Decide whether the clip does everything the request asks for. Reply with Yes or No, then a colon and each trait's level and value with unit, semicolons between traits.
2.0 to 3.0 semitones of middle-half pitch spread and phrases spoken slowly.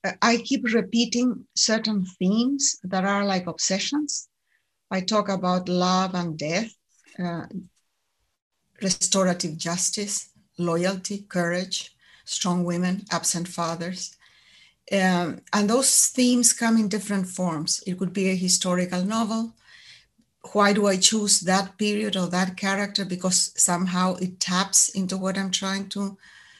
Yes: narrow, 2.4 semitones; slow, 125 wpm